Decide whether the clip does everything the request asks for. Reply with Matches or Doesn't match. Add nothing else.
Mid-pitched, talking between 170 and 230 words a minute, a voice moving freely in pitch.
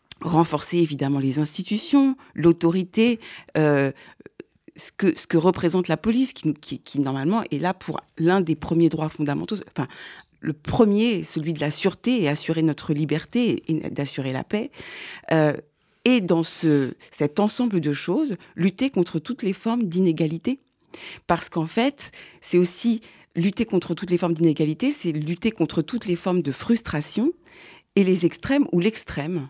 Doesn't match